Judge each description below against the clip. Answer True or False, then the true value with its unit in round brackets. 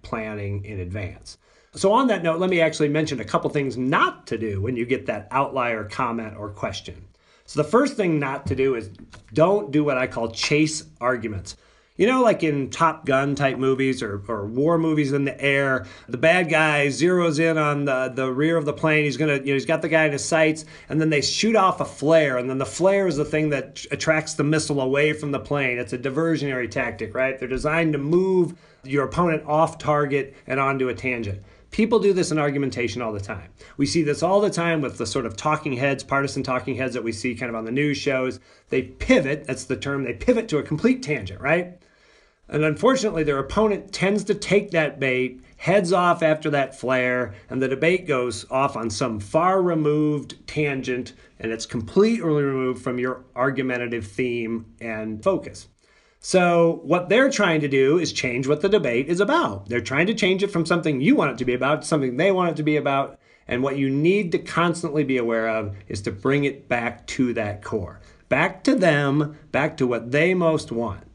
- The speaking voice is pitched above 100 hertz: True (140 Hz)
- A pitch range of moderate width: True (4.3 semitones)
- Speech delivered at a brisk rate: True (215 wpm)